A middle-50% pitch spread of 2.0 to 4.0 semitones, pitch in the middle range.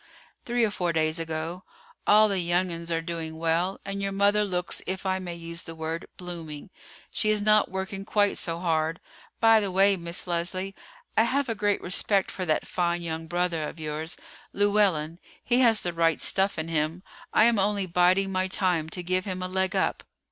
Yes: average, 3.0 semitones; medium, 180 Hz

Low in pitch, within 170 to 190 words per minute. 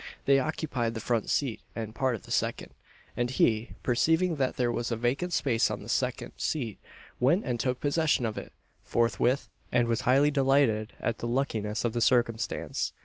Yes: low, 120 Hz; average, 185 wpm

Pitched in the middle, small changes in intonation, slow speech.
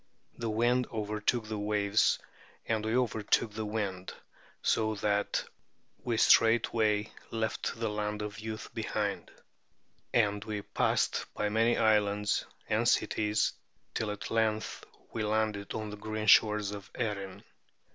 No: low, 105 Hz; narrow, 1.2 semitones; slow, 130 wpm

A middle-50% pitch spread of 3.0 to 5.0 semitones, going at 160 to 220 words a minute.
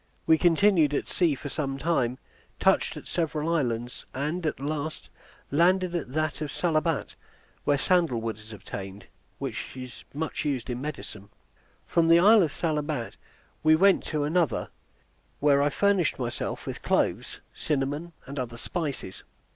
No: average, 4.4 semitones; average, 150 wpm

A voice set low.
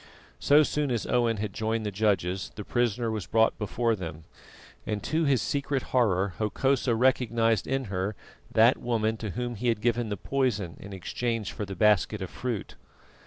Yes: low, 110 Hz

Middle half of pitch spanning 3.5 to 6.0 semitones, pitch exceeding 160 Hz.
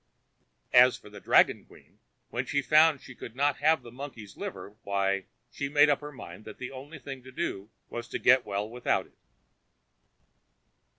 No: average, 5.2 semitones; low, 130 Hz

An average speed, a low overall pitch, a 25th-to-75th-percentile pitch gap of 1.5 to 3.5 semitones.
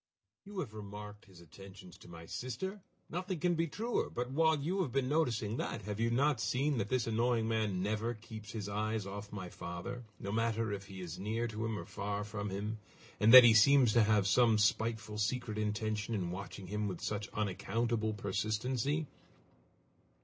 Yes: average, 185 wpm; low, 110 Hz; average, 3.2 semitones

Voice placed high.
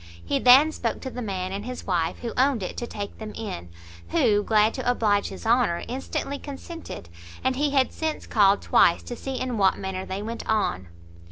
Yes: high, 225 Hz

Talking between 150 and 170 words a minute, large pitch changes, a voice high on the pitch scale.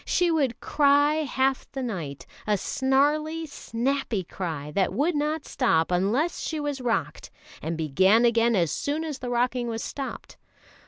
Yes: average, 155 wpm; wide, 6.5 semitones; very high, 250 Hz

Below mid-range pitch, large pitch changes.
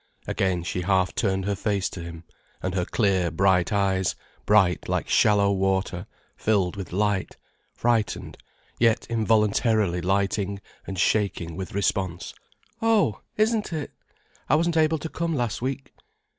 No: low, 100 Hz; average, 3.3 semitones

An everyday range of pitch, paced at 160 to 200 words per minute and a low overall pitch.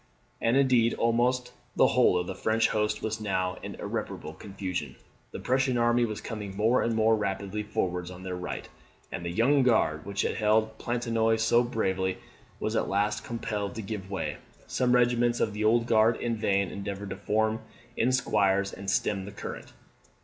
Yes: average, 3.1 semitones; average, 180 wpm; low, 110 Hz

